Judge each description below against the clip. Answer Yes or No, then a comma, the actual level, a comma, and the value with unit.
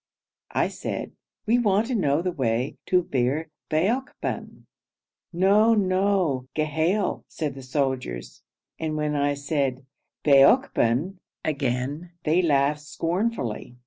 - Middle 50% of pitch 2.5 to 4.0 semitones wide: No, average, 5.3 semitones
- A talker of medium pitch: Yes, medium, 155 Hz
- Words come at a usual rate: No, slow, 110 wpm